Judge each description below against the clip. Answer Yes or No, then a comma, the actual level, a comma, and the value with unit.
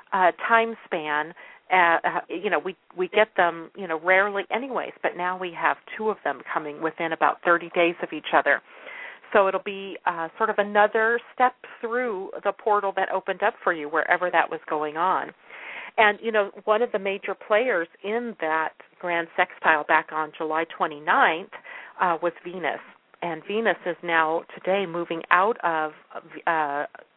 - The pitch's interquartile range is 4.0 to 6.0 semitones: Yes, average, 4.3 semitones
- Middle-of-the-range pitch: Yes, medium, 180 Hz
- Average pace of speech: Yes, average, 170 wpm